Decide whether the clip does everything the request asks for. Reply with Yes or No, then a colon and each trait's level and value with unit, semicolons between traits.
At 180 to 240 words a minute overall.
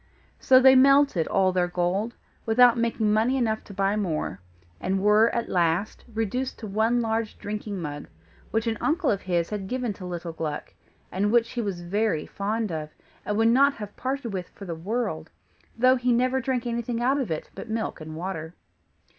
Yes: average, 190 wpm